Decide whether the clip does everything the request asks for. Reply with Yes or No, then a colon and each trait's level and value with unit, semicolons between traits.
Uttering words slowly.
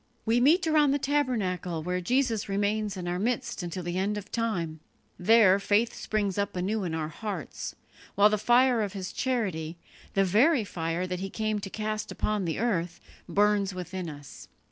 No: average, 180 wpm